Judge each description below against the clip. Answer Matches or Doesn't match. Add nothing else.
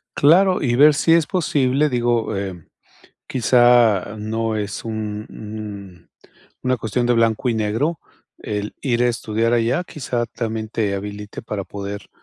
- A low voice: Matches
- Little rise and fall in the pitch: Doesn't match